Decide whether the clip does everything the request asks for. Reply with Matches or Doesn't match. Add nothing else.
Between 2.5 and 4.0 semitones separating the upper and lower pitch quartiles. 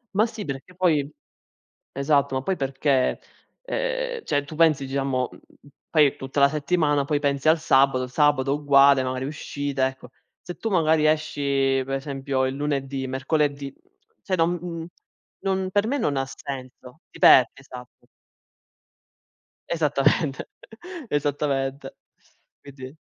Matches